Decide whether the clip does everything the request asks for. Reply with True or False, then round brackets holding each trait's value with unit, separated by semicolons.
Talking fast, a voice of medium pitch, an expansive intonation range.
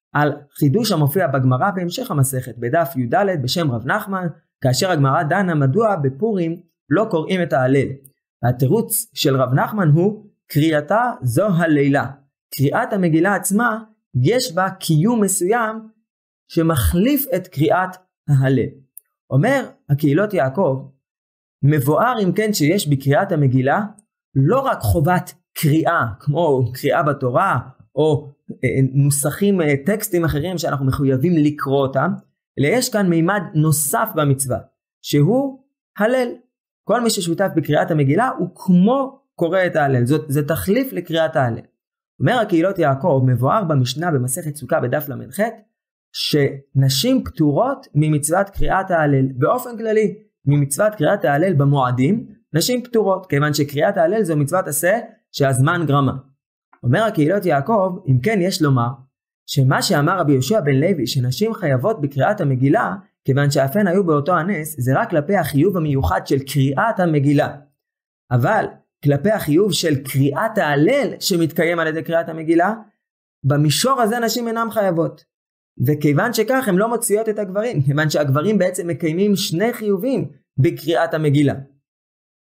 False (130 wpm; 160 Hz; 6.2 semitones)